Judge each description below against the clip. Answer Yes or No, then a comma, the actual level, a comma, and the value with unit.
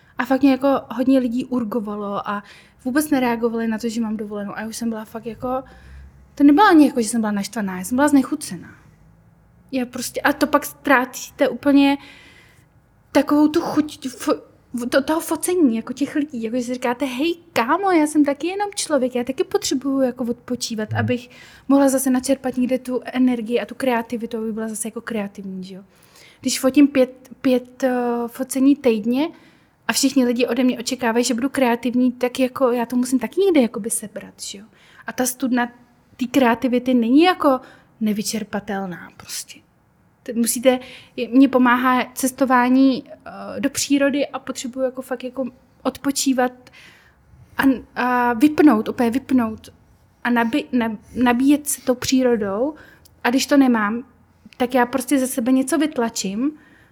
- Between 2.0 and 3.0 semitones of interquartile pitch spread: Yes, narrow, 2.6 semitones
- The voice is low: No, very high, 255 Hz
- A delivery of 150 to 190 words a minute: Yes, average, 160 wpm